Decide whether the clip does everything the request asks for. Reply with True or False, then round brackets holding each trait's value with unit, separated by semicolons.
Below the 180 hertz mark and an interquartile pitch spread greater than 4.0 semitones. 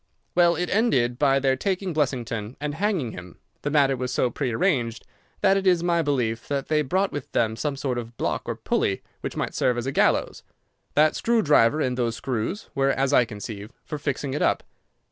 True (135 Hz; 4.6 semitones)